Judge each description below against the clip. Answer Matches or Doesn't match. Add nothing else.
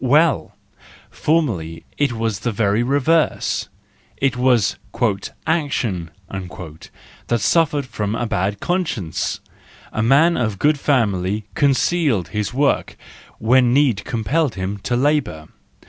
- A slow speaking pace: Matches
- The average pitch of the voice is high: Doesn't match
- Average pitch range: Doesn't match